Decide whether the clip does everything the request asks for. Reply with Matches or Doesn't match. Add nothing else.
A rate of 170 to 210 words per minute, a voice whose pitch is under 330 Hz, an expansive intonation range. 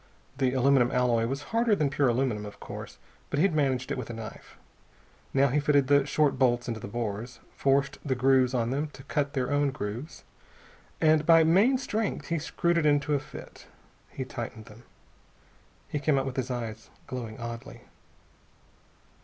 Doesn't match